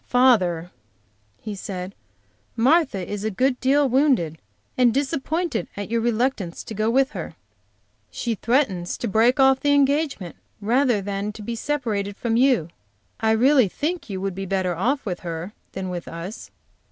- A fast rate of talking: No, average, 160 wpm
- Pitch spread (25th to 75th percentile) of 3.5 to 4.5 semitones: No, wide, 5.6 semitones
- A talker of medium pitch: No, high, 225 Hz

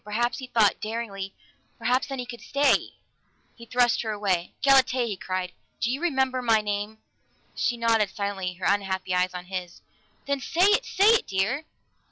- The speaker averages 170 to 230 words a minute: Yes, average, 175 wpm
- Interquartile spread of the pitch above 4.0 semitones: Yes, average, 4.8 semitones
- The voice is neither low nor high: No, high, 225 Hz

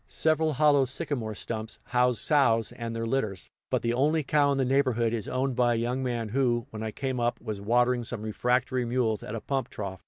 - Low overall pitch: Yes, low, 120 Hz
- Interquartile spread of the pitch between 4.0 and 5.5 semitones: No, average, 2.9 semitones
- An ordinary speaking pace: No, fast, 215 wpm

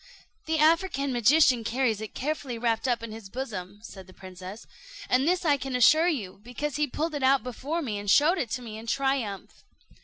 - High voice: Yes, very high, 250 Hz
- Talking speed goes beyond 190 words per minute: Yes, fast, 205 wpm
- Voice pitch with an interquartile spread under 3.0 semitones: No, average, 5.1 semitones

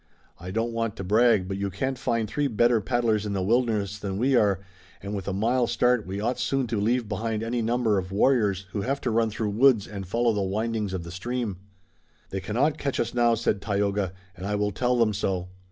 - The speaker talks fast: Yes, fast, 230 wpm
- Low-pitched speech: Yes, low, 110 Hz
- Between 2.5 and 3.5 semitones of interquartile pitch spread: Yes, average, 3.2 semitones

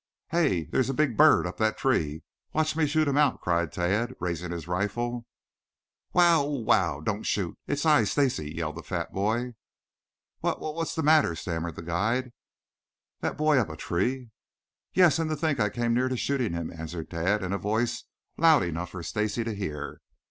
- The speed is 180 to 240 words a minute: Yes, average, 185 wpm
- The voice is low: Yes, low, 110 Hz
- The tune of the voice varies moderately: No, wide, 8.3 semitones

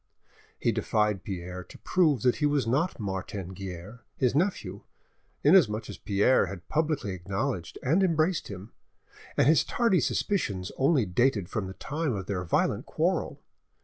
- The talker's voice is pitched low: Yes, low, 110 Hz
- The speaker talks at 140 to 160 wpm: Yes, average, 150 wpm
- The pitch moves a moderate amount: No, wide, 7.9 semitones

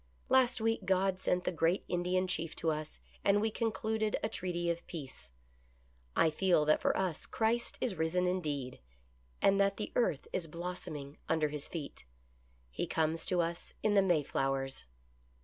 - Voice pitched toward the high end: No, medium, 175 Hz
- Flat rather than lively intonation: No, average, 4.1 semitones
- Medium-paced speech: Yes, average, 165 wpm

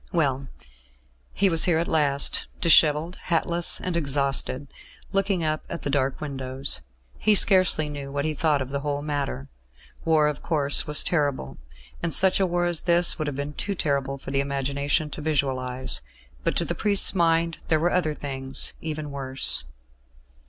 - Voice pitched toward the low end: No, medium, 150 Hz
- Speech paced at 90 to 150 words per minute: No, average, 170 wpm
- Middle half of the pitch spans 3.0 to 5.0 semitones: Yes, average, 3.4 semitones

